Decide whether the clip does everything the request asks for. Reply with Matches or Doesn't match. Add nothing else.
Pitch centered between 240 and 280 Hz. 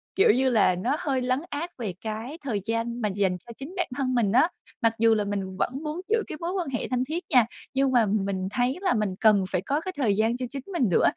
Matches